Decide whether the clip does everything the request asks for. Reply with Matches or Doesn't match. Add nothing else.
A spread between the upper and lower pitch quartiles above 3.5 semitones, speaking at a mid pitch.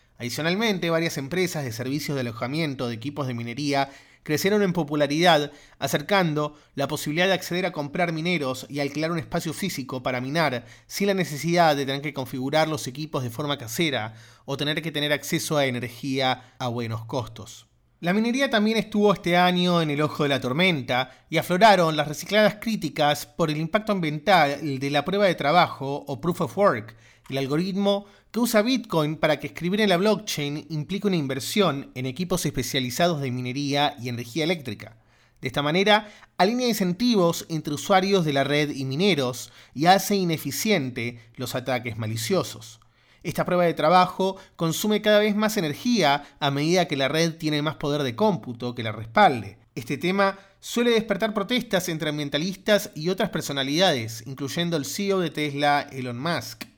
Matches